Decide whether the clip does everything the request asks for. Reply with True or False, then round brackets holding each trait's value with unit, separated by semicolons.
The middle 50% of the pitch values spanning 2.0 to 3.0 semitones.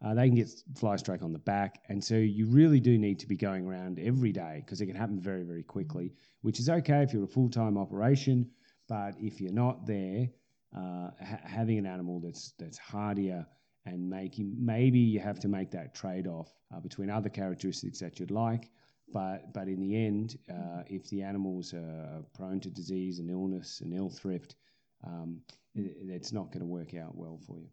False (3.5 semitones)